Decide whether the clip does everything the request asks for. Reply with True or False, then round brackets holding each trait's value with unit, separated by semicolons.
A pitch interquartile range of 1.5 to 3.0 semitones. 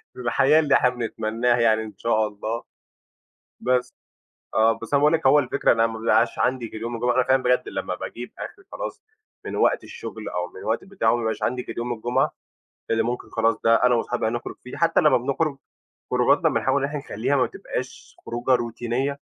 True (2.7 semitones)